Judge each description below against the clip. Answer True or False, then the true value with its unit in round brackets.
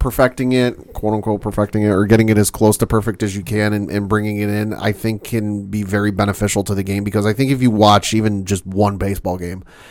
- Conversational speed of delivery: False (250 wpm)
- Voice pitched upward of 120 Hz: False (105 Hz)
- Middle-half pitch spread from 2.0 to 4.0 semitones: False (1.3 semitones)